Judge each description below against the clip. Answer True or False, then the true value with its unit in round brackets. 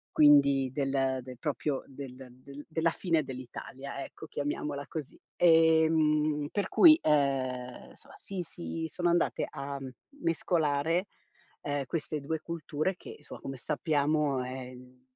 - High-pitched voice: False (145 Hz)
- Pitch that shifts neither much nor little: True (3.1 semitones)